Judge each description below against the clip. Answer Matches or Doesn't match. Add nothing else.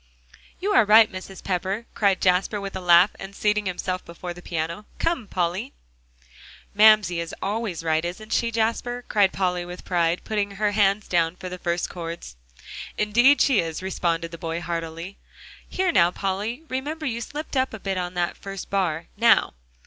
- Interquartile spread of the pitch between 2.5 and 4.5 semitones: Matches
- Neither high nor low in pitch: Doesn't match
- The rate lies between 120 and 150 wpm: Doesn't match